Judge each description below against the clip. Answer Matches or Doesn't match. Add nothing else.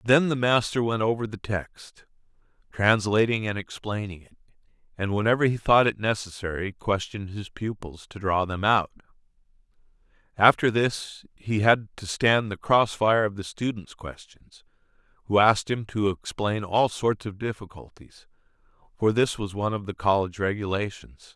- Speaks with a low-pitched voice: Matches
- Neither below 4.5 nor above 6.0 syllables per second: Matches